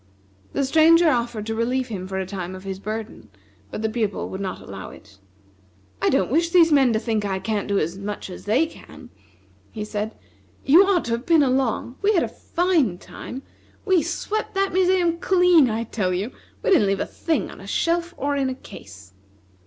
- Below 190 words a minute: No, fast, 205 wpm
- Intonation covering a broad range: Yes, wide, 8.7 semitones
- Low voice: No, high, 240 Hz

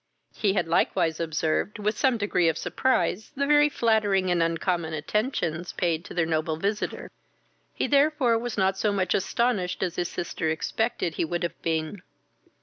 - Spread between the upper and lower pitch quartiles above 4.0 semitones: Yes, average, 4.9 semitones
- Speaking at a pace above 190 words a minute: No, average, 165 wpm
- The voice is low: No, medium, 185 Hz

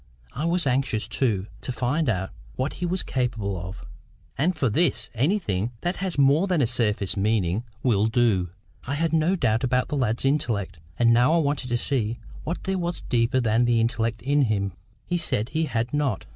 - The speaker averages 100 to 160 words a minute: No, average, 195 wpm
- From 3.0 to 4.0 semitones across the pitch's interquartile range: No, average, 5.3 semitones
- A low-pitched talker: Yes, low, 125 Hz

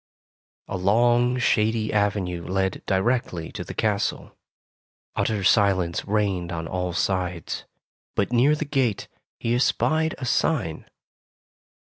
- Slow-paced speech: Yes, slow, 115 wpm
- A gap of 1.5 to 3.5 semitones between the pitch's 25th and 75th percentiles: No, average, 4.8 semitones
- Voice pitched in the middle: No, low, 105 Hz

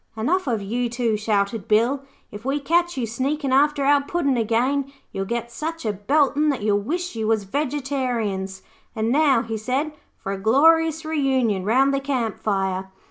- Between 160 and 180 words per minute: Yes, average, 175 wpm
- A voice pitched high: Yes, very high, 250 Hz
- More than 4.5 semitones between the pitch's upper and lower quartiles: Yes, average, 4.9 semitones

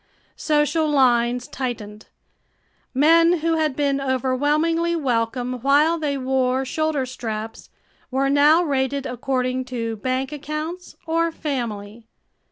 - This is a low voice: No, very high, 270 Hz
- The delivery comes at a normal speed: No, slow, 110 wpm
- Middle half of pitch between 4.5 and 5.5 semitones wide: No, average, 3.4 semitones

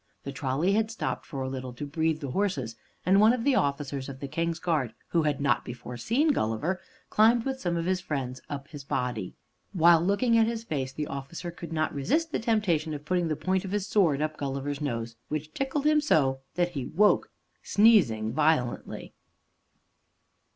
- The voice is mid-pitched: Yes, medium, 155 Hz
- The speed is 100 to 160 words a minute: No, average, 185 wpm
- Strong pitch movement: Yes, wide, 6.3 semitones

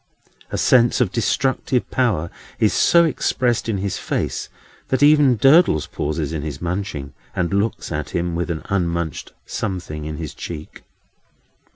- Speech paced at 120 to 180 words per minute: Yes, average, 150 wpm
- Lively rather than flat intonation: Yes, wide, 7.5 semitones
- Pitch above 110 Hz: No, very low, 90 Hz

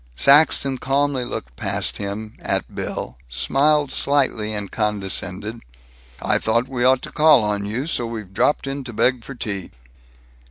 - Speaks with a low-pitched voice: Yes, low, 120 Hz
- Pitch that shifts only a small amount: No, average, 4.7 semitones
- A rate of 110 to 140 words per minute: No, average, 155 wpm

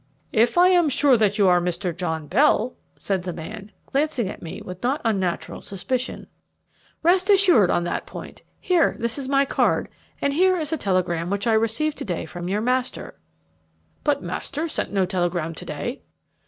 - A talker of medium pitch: No, high, 220 Hz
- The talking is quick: No, average, 185 wpm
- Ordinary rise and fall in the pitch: No, wide, 7.9 semitones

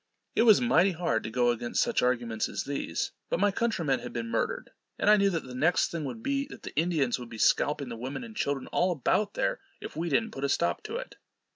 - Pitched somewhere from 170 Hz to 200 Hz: No, medium, 155 Hz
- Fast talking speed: Yes, fast, 245 wpm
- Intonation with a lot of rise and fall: Yes, wide, 8.6 semitones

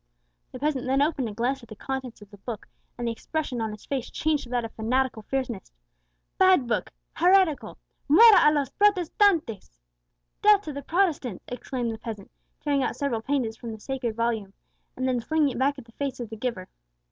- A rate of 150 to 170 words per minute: No, average, 200 wpm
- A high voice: Yes, very high, 255 Hz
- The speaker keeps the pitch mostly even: No, average, 4.3 semitones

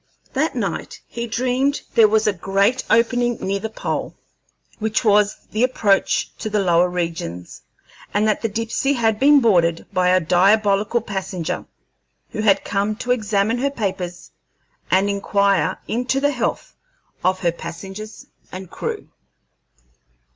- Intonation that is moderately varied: Yes, average, 3.5 semitones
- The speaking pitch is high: Yes, high, 210 Hz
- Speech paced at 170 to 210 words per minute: No, average, 145 wpm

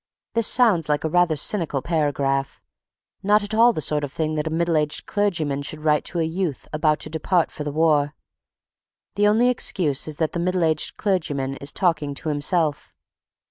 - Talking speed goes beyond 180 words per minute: Yes, average, 190 wpm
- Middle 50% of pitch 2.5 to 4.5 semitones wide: Yes, average, 3.5 semitones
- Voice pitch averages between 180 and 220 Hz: No, medium, 160 Hz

